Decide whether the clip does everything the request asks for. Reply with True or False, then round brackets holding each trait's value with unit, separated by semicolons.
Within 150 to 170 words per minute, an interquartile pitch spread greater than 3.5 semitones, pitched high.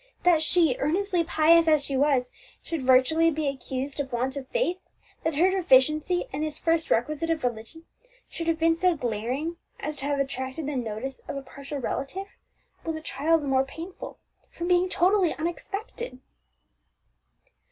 True (165 wpm; 3.9 semitones; 310 Hz)